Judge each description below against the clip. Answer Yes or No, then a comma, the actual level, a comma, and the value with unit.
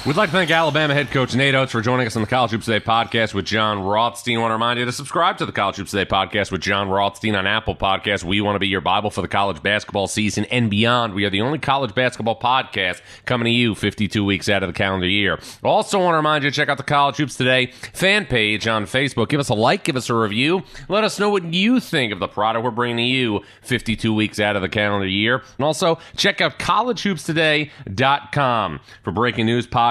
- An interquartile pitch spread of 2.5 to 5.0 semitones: No, wide, 5.6 semitones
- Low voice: Yes, low, 115 Hz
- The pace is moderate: No, fast, 245 wpm